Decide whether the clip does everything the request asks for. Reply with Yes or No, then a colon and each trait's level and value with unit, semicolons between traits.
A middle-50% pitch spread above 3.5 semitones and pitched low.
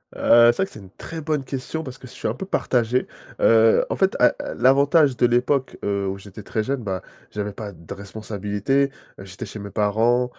Yes: average, 4.6 semitones; low, 115 Hz